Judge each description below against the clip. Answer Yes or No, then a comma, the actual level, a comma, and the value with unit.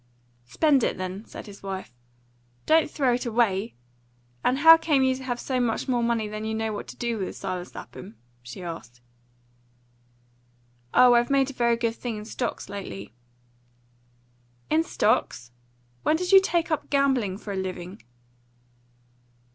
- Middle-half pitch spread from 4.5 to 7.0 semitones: Yes, average, 5.3 semitones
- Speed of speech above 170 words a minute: No, average, 160 wpm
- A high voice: Yes, high, 235 Hz